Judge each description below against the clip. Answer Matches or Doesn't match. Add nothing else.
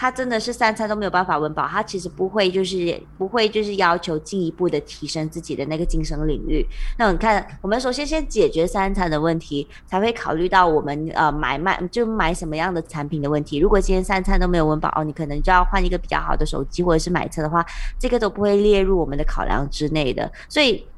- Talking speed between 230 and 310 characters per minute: Doesn't match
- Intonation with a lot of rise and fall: Doesn't match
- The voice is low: Doesn't match